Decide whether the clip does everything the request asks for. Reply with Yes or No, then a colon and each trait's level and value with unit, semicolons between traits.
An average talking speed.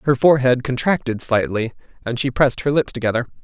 Yes: average, 175 wpm